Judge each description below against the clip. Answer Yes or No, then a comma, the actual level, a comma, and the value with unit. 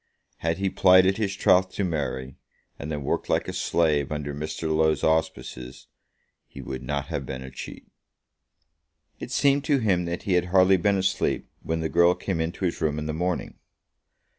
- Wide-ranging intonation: No, average, 3.9 semitones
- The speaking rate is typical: Yes, average, 185 wpm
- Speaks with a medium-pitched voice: No, very low, 80 Hz